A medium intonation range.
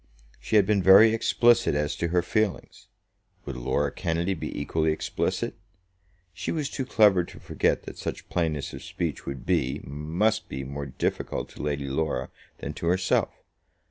No: wide, 6.0 semitones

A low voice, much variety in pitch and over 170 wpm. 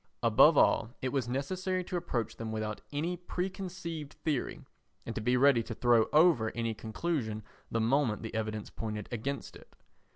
No: low, 125 Hz; wide, 6.7 semitones; average, 165 wpm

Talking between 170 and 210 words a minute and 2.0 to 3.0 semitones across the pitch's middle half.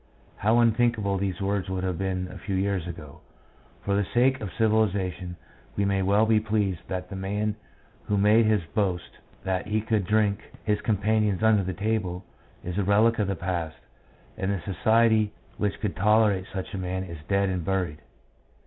Yes: average, 180 wpm; narrow, 2.5 semitones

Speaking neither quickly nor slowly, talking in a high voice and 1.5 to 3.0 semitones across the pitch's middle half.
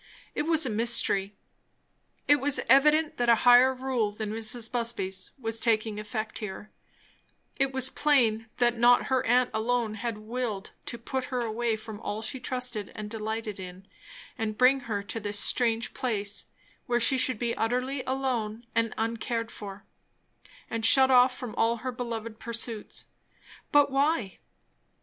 Yes: average, 155 wpm; high, 230 Hz; average, 2.7 semitones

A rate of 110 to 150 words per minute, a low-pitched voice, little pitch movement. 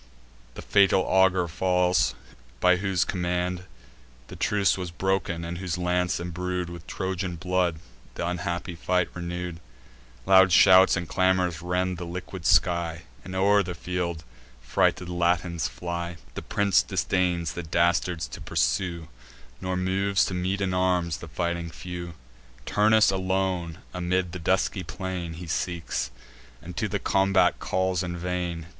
Yes: average, 145 wpm; very low, 90 Hz; narrow, 1.3 semitones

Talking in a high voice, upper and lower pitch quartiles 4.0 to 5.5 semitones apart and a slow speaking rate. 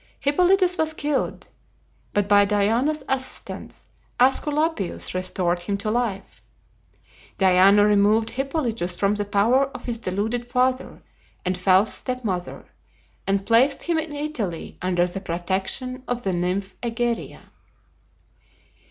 Yes: high, 215 Hz; average, 5.2 semitones; slow, 115 wpm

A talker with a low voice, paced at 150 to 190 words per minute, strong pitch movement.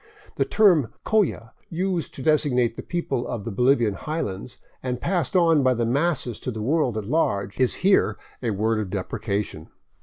Yes: low, 125 Hz; average, 180 wpm; wide, 6.6 semitones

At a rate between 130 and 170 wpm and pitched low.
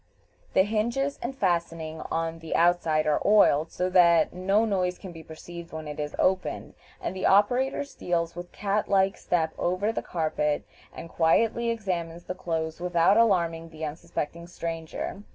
No: average, 160 wpm; medium, 175 Hz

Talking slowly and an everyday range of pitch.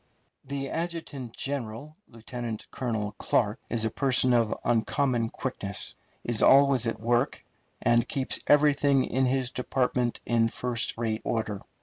Yes: slow, 130 wpm; average, 3.1 semitones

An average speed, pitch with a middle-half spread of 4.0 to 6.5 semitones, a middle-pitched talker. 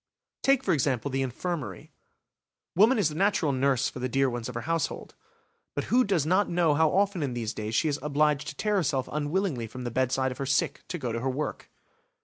No: fast, 220 wpm; average, 5.1 semitones; medium, 145 Hz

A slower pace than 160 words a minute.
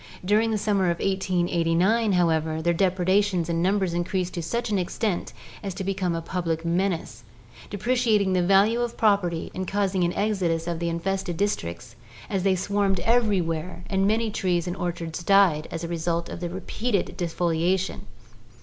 No: average, 170 wpm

